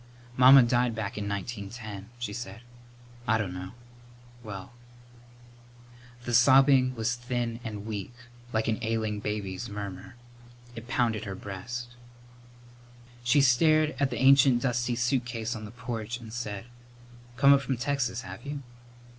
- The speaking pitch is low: Yes, low, 120 Hz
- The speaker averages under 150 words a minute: Yes, average, 140 wpm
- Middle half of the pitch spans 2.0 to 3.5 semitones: Yes, average, 2.7 semitones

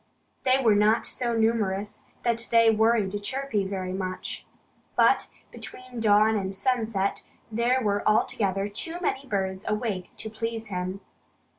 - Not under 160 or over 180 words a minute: No, slow, 135 wpm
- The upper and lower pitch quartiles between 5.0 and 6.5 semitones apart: No, average, 2.8 semitones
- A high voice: Yes, high, 215 Hz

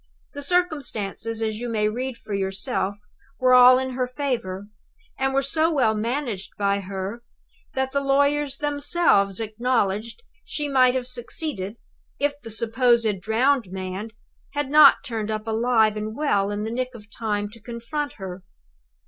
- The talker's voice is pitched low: No, high, 235 Hz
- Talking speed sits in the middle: Yes, average, 155 wpm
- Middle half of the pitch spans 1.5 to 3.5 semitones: No, average, 4.4 semitones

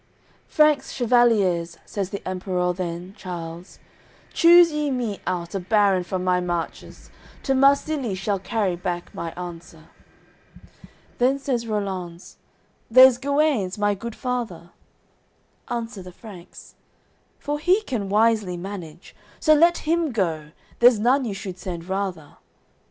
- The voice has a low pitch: No, high, 200 Hz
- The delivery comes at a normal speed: No, slow, 130 wpm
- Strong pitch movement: Yes, wide, 5.8 semitones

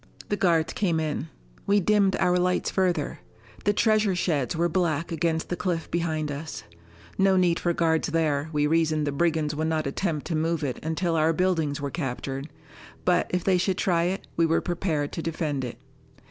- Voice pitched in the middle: Yes, medium, 165 Hz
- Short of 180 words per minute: No, average, 190 wpm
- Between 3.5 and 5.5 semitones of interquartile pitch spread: No, average, 2.7 semitones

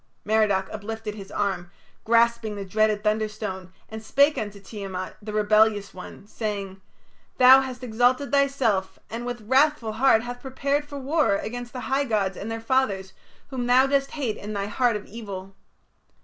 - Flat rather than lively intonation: No, average, 3.8 semitones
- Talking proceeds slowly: No, average, 165 wpm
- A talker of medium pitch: No, high, 220 Hz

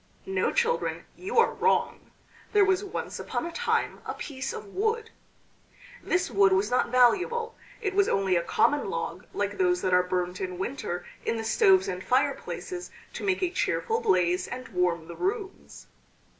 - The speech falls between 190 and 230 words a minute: No, average, 170 wpm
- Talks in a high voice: Yes, very high, 330 Hz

